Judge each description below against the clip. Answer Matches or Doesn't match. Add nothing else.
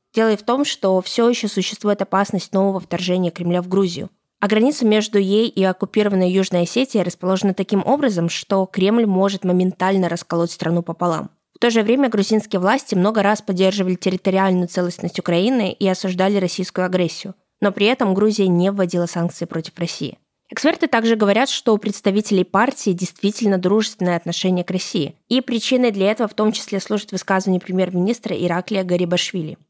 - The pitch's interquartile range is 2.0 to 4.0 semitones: Matches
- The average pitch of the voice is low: Doesn't match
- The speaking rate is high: Matches